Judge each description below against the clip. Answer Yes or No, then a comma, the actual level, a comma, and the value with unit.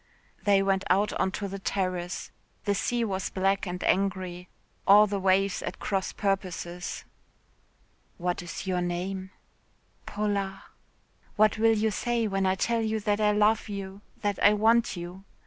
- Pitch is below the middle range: No, high, 195 Hz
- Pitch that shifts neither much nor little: No, narrow, 1.9 semitones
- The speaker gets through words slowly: No, average, 155 wpm